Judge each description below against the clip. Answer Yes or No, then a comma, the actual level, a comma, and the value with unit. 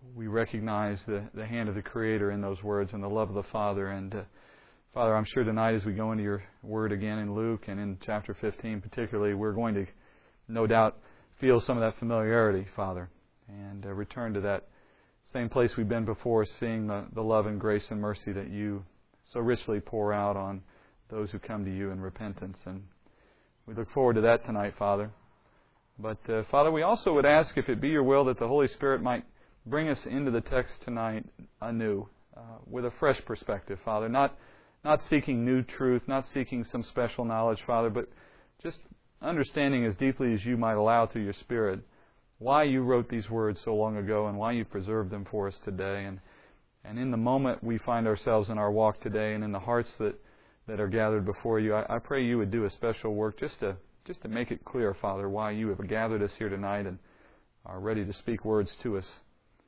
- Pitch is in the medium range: No, low, 110 Hz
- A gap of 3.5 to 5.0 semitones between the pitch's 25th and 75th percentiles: No, narrow, 2.4 semitones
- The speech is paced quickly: Yes, fast, 210 wpm